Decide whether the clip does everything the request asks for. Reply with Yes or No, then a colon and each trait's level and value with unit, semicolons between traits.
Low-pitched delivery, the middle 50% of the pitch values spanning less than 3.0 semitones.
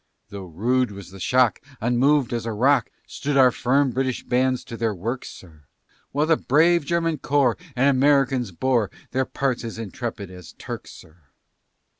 No: low, 125 Hz; average, 3.8 semitones